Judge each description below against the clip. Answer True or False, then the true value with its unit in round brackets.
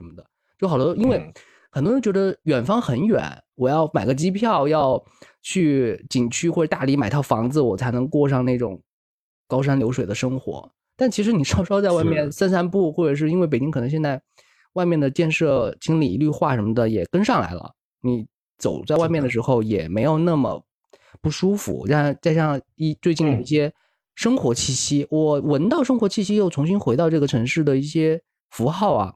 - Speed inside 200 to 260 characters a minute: False (290 characters per minute)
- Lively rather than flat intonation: False (4.8 semitones)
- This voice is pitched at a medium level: True (150 Hz)